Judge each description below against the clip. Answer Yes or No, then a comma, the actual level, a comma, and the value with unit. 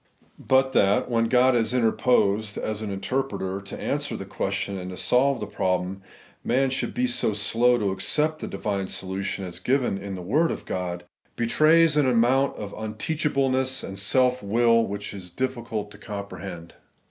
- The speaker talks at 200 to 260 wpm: No, average, 175 wpm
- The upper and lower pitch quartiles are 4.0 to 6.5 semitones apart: Yes, average, 4.9 semitones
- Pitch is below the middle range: Yes, low, 110 Hz